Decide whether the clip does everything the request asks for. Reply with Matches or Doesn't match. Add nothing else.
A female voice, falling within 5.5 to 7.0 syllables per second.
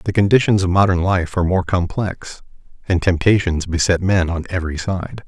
Doesn't match